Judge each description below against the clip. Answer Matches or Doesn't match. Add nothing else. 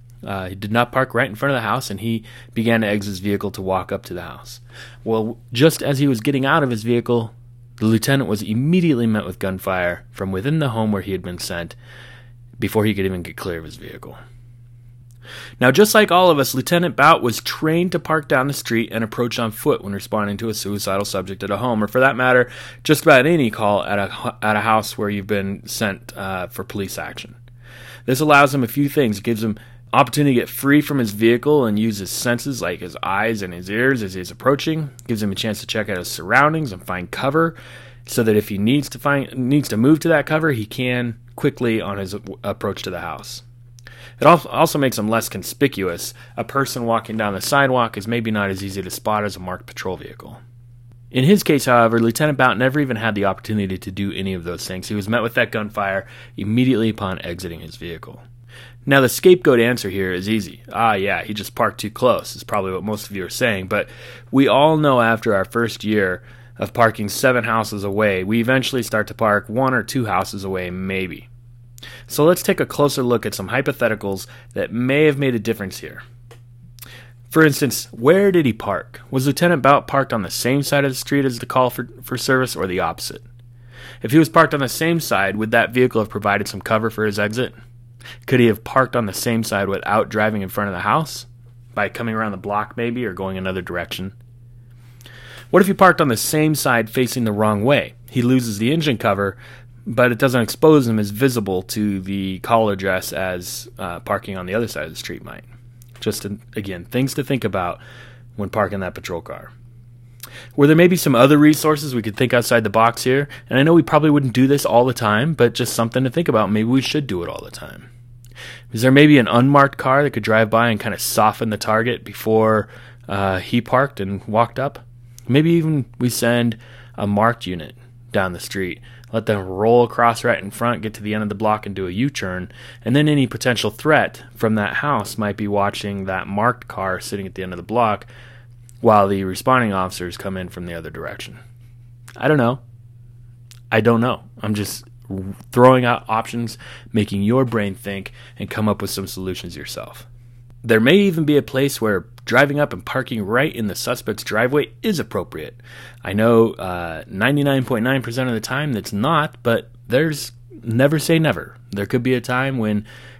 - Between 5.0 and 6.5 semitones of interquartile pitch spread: Doesn't match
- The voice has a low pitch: Matches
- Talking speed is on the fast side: Matches